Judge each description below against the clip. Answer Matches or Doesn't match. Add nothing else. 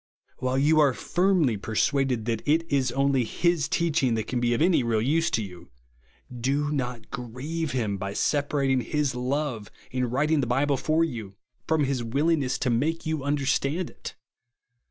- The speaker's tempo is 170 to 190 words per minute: Matches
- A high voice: Doesn't match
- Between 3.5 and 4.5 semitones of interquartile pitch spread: Matches